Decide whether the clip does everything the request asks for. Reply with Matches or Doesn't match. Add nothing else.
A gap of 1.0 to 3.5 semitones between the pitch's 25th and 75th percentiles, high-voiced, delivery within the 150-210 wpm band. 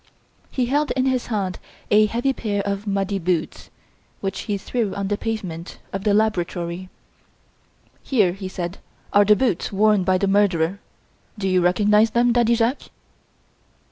Matches